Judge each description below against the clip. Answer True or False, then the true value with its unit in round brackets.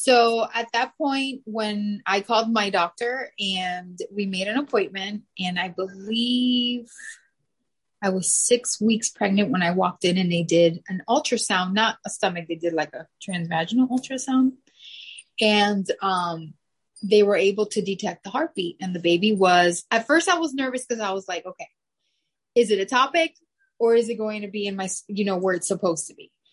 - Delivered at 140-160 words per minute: False (185 wpm)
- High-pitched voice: True (205 Hz)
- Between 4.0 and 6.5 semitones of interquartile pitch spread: True (4.5 semitones)